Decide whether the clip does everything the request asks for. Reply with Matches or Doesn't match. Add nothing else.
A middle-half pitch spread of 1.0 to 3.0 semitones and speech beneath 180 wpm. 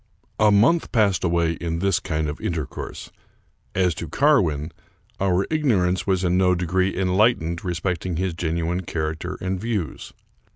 Matches